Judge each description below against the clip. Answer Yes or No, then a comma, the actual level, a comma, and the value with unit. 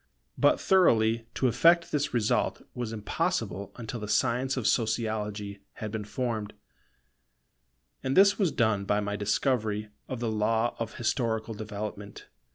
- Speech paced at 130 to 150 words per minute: Yes, average, 140 wpm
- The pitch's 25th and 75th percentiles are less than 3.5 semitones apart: Yes, average, 2.8 semitones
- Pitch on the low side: Yes, low, 110 Hz